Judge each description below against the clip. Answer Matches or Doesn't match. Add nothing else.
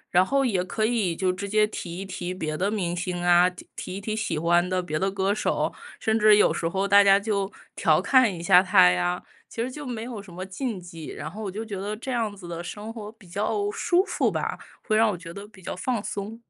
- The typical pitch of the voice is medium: Doesn't match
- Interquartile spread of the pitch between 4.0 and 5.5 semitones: Doesn't match